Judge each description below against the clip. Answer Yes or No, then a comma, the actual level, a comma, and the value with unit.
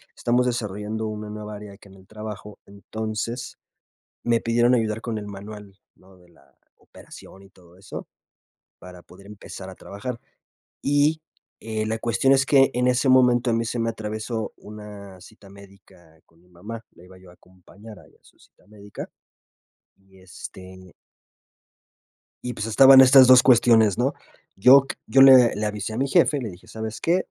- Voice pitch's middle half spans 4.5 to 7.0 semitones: No, average, 3.7 semitones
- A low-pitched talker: Yes, low, 110 Hz